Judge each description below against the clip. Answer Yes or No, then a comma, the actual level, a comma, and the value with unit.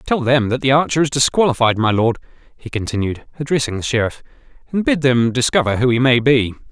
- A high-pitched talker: No, low, 130 Hz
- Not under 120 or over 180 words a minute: No, average, 195 wpm